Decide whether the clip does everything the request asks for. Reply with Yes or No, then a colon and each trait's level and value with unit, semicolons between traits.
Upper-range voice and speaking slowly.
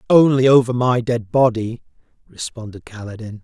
No: low, 120 Hz; slow, 120 wpm